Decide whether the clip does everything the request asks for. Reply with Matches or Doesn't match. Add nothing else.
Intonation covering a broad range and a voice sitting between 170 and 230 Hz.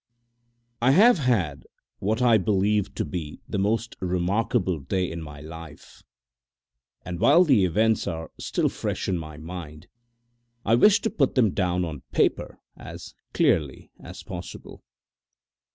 Doesn't match